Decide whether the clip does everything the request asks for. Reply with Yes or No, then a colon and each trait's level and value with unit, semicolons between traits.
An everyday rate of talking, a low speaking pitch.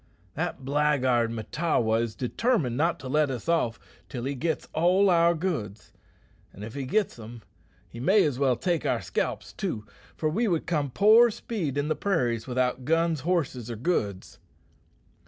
No: average, 170 wpm; medium, 145 Hz